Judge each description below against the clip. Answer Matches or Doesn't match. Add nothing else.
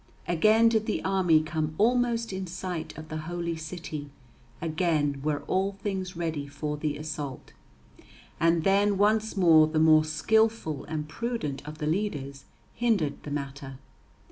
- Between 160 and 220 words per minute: Doesn't match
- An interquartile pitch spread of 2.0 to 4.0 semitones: Doesn't match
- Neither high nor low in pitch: Matches